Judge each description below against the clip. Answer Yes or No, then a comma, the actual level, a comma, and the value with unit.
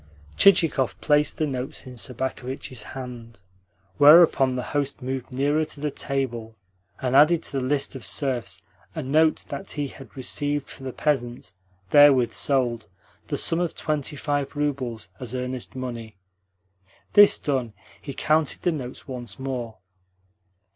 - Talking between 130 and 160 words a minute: Yes, average, 145 wpm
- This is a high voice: No, low, 135 Hz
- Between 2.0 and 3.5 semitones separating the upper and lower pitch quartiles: Yes, average, 2.8 semitones